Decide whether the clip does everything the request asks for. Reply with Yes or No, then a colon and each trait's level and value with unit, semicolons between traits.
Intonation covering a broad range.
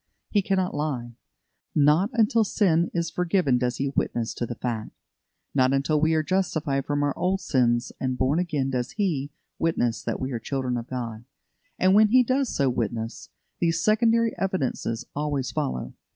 Yes: wide, 6.7 semitones